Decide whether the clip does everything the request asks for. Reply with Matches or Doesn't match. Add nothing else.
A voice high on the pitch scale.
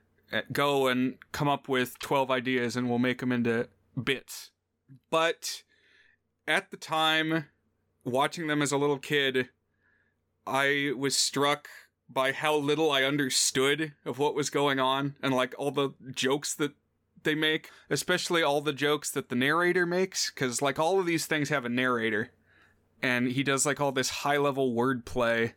Doesn't match